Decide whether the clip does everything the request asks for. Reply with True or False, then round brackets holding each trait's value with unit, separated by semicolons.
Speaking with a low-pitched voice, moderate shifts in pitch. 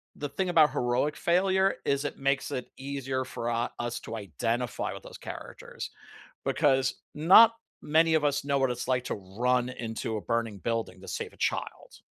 True (130 Hz; 3.8 semitones)